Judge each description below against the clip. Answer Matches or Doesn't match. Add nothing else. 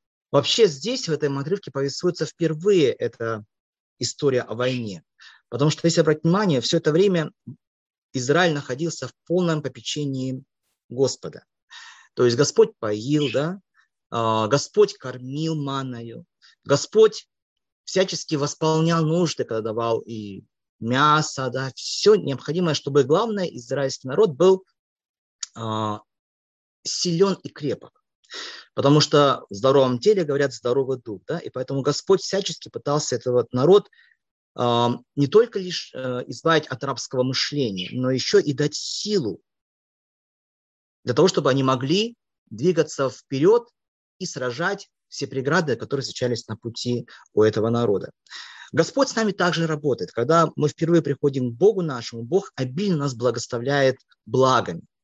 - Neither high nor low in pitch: Matches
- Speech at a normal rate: Matches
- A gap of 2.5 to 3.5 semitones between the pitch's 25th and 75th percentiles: Doesn't match